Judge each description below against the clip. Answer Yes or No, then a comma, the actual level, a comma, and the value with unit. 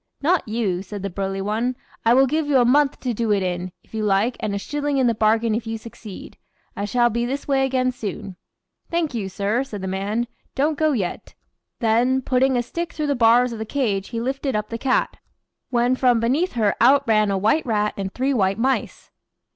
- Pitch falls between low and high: No, high, 235 Hz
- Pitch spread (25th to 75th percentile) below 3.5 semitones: No, average, 4.1 semitones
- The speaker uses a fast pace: Yes, fast, 220 wpm